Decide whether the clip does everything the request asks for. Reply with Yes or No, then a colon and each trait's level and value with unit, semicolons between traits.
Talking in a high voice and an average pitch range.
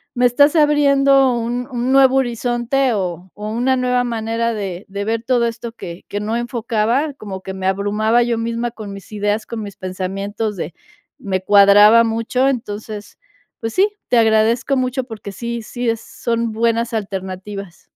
Yes: high, 230 Hz; average, 3.1 semitones